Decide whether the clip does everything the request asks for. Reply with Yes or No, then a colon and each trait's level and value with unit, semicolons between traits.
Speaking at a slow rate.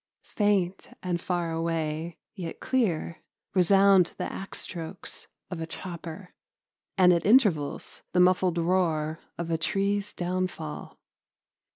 Yes: slow, 115 wpm